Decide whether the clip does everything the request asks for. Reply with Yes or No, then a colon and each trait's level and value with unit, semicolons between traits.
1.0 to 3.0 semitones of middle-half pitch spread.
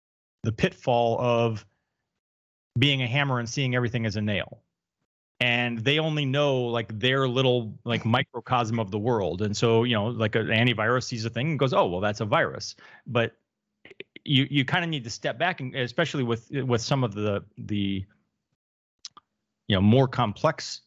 No: average, 3.5 semitones